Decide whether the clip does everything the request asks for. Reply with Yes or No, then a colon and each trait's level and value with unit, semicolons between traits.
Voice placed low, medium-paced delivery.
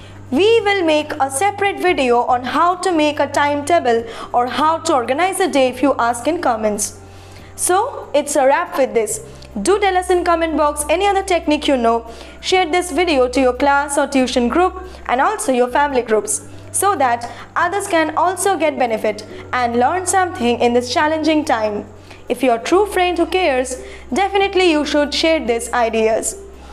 No: very high, 295 Hz; average, 180 wpm